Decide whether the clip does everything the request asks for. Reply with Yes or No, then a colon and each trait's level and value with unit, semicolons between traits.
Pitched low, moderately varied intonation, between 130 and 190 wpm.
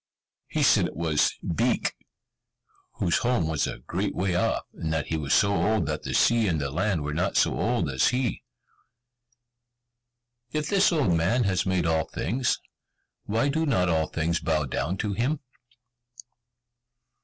No: very low, 90 Hz; wide, 6.4 semitones; average, 165 wpm